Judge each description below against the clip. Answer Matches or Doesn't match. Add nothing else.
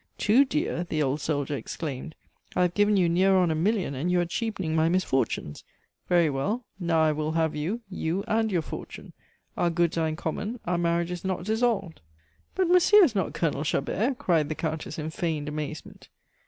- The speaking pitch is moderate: Matches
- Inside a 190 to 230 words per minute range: Matches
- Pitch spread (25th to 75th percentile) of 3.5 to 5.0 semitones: Matches